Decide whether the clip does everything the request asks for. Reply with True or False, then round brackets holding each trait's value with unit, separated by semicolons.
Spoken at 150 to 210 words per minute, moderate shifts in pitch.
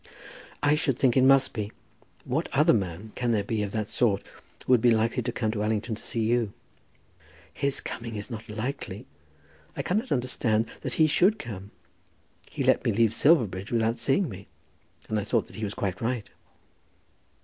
True (185 wpm; 3.3 semitones)